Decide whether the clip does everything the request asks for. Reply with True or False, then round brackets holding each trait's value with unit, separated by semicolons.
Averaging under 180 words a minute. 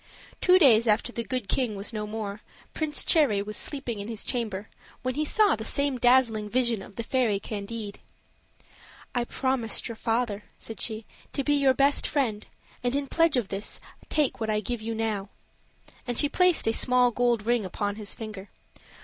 False (185 wpm)